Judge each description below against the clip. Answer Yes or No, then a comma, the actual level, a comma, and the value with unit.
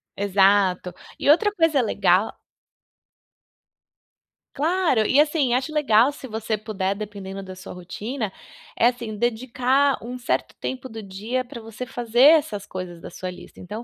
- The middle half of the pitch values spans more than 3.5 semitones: Yes, average, 4.6 semitones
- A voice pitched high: Yes, high, 225 Hz